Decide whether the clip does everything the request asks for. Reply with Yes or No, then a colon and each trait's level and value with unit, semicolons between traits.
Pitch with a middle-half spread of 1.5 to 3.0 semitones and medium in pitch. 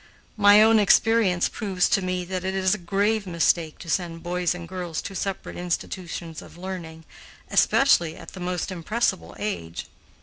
Yes: narrow, 2.5 semitones; medium, 180 Hz